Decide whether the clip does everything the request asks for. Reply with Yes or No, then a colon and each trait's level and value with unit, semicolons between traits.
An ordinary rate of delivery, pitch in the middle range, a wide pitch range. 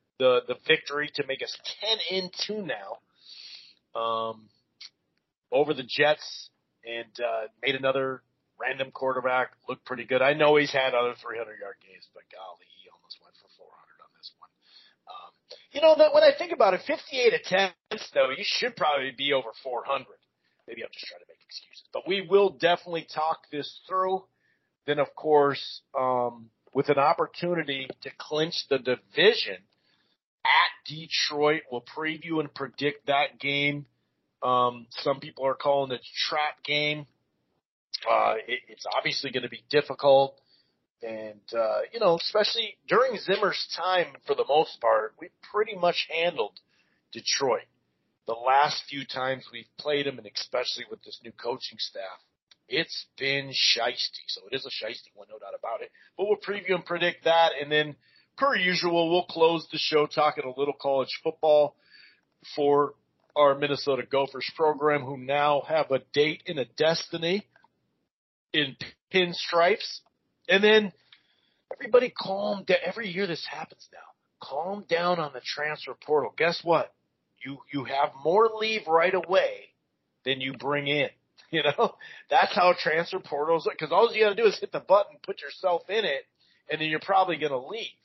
Yes: average, 170 wpm; medium, 155 Hz; wide, 5.9 semitones